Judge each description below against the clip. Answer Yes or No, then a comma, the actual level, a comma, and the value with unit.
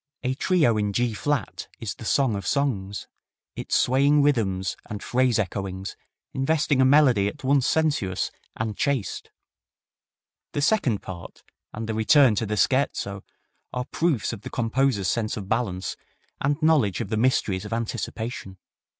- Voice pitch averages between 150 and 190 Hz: No, low, 115 Hz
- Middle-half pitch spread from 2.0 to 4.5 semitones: No, average, 5.2 semitones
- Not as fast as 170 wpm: Yes, average, 150 wpm